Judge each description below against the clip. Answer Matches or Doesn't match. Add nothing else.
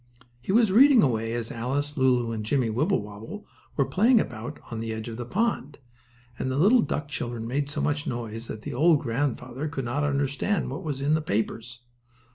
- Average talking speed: Matches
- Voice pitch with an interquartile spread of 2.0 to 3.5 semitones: Doesn't match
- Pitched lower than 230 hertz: Matches